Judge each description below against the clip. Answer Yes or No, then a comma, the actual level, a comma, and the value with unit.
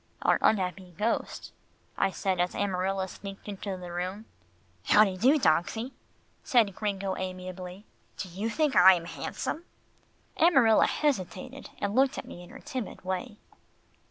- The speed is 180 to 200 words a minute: No, average, 145 wpm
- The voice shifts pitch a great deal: No, average, 3.4 semitones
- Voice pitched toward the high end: Yes, high, 195 Hz